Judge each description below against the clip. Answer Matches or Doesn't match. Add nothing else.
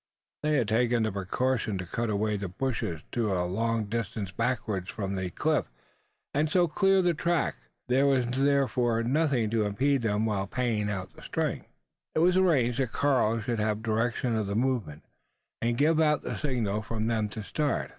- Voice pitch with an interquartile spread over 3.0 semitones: Matches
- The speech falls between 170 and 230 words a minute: Matches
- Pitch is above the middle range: Doesn't match